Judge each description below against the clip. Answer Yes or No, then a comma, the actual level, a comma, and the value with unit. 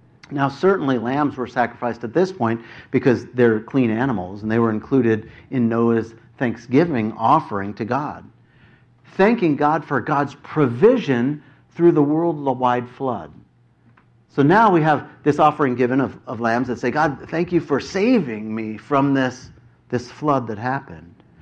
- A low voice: Yes, low, 125 Hz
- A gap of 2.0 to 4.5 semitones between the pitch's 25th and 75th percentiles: Yes, average, 4.1 semitones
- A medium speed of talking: Yes, average, 155 wpm